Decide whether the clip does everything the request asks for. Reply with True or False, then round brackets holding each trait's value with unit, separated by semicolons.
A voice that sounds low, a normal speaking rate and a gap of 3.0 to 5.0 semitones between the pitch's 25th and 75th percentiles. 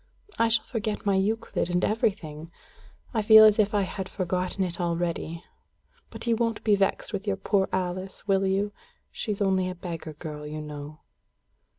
False (190 Hz; 180 wpm; 3.4 semitones)